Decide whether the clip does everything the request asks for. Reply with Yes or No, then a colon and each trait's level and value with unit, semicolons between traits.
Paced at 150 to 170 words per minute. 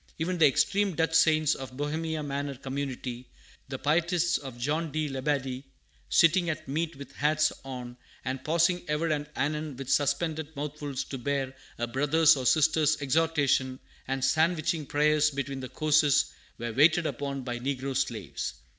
Yes: average, 155 wpm